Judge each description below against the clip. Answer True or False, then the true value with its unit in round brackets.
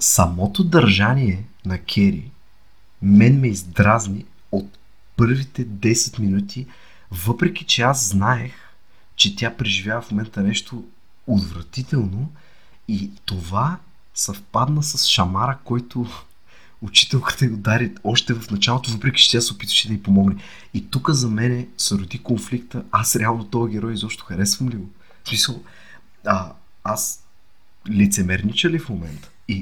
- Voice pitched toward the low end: True (110 Hz)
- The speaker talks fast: False (125 wpm)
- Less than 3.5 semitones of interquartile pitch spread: False (3.9 semitones)